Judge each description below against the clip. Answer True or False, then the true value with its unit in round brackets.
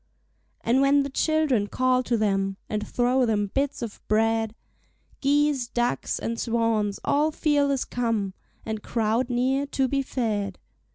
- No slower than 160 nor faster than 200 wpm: False (145 wpm)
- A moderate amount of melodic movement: True (4.0 semitones)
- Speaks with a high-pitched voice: True (240 Hz)